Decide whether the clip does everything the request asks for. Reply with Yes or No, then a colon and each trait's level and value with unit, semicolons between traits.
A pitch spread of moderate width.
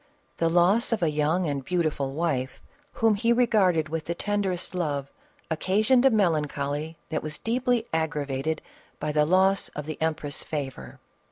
Yes: average, 4.7 semitones